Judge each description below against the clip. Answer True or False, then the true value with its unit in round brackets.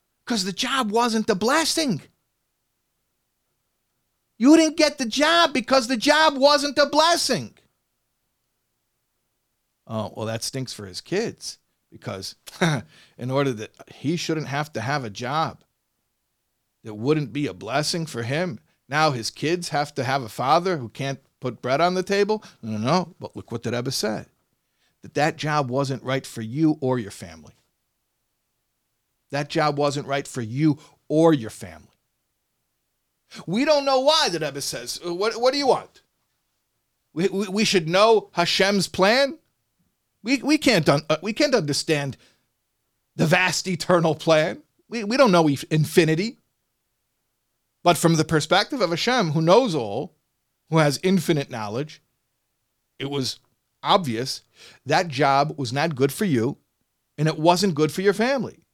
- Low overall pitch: False (155 Hz)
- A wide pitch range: True (7.4 semitones)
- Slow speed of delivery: False (150 wpm)